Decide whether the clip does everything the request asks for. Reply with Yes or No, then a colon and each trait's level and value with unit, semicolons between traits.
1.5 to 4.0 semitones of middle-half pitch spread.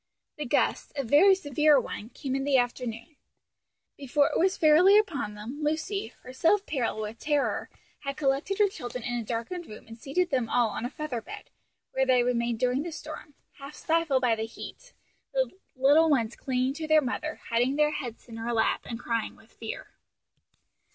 No: average, 4.4 semitones